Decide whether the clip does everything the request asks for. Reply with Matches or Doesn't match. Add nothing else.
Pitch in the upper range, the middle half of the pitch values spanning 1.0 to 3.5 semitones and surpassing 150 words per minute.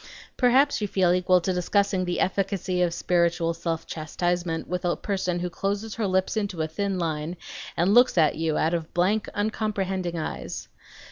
Doesn't match